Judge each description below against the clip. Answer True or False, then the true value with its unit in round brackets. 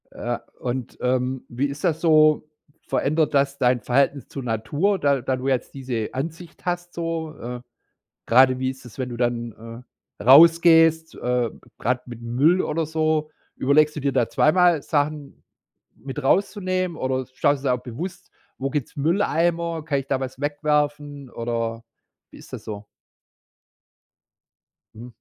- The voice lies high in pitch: False (140 Hz)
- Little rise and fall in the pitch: False (4.2 semitones)